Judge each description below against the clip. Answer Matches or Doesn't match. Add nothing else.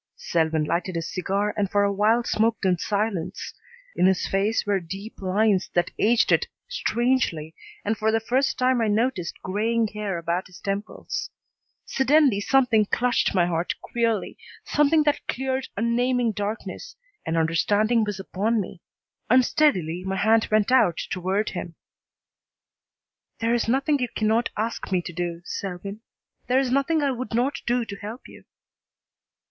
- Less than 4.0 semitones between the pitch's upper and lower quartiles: Doesn't match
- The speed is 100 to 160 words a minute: Matches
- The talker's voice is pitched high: Matches